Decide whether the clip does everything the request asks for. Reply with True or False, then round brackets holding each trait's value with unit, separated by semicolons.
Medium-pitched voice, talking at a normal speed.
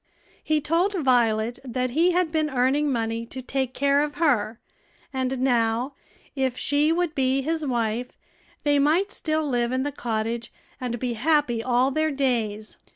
False (260 Hz; 160 wpm)